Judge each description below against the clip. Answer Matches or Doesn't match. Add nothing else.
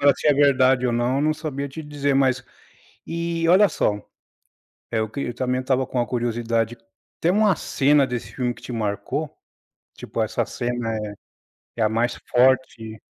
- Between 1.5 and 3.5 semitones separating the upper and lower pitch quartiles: Matches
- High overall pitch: Doesn't match